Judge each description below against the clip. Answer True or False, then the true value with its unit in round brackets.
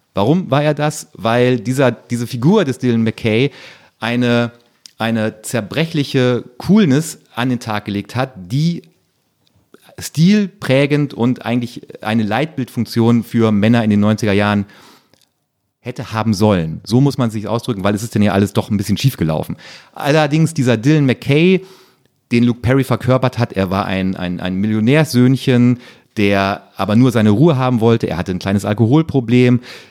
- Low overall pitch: True (120 Hz)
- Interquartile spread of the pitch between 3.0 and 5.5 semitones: True (3.7 semitones)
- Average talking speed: True (155 wpm)